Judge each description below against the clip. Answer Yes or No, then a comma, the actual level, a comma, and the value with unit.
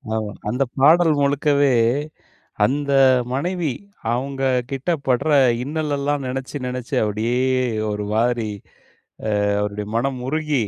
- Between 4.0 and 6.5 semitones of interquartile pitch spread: No, average, 3.0 semitones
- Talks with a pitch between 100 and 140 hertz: Yes, low, 135 Hz